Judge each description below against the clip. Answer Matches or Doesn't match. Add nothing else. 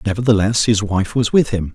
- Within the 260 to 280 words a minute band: Doesn't match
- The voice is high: Doesn't match